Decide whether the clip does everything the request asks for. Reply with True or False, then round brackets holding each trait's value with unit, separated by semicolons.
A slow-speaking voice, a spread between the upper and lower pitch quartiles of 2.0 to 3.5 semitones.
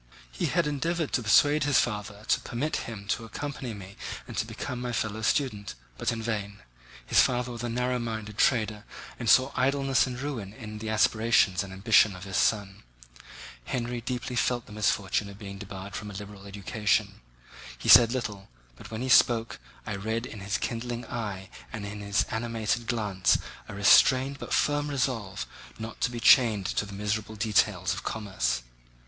False (180 wpm; 3.2 semitones)